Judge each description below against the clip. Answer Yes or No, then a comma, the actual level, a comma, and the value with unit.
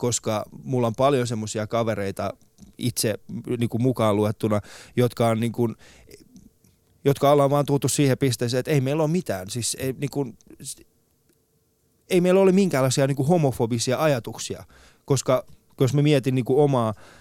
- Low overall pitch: Yes, low, 125 Hz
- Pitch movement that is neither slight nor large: Yes, average, 3.7 semitones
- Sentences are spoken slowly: No, fast, 155 wpm